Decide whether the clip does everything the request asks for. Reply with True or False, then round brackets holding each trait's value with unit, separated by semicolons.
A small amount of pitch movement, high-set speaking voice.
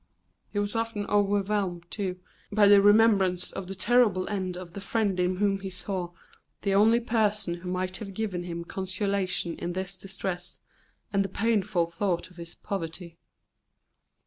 True (2.3 semitones; 195 Hz)